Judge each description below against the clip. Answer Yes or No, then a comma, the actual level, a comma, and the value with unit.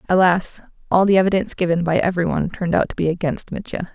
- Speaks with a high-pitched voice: No, medium, 180 Hz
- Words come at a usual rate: No, fast, 215 wpm